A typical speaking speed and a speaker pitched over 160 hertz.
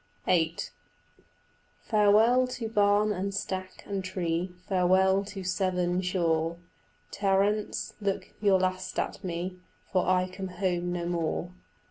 No: slow, 120 wpm; medium, 185 Hz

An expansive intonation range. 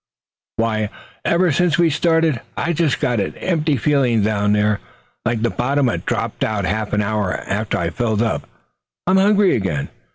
Yes: wide, 7.2 semitones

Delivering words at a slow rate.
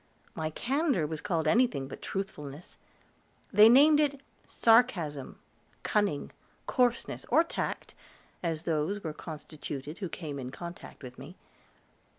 Yes: slow, 125 wpm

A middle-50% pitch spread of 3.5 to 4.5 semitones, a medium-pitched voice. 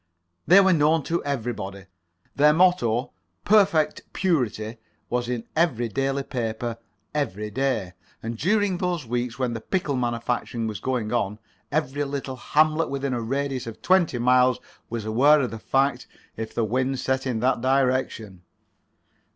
No: average, 3.9 semitones; low, 130 Hz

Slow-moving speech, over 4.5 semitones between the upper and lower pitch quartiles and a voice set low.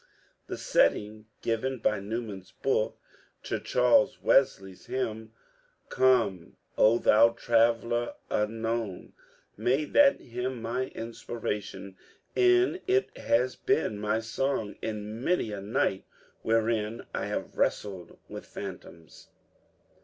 No: slow, 115 wpm; average, 3.1 semitones; low, 115 Hz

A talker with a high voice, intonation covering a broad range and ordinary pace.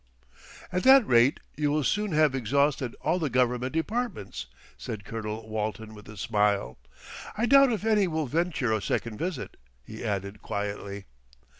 No: low, 125 Hz; wide, 7.8 semitones; average, 155 wpm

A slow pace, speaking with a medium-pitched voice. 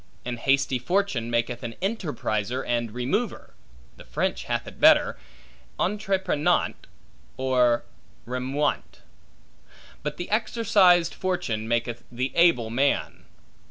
No: slow, 105 wpm; low, 130 Hz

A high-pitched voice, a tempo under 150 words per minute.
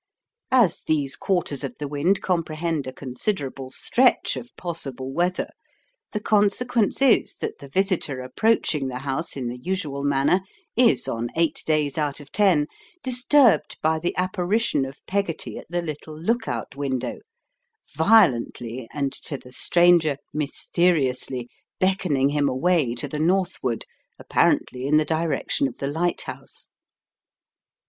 No: medium, 155 Hz; average, 140 wpm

